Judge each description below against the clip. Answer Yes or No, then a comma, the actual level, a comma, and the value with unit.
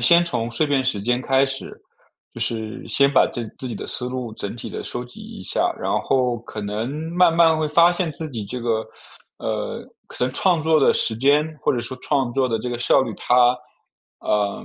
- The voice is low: Yes, low, 125 Hz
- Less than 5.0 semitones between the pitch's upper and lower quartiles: Yes, average, 3.5 semitones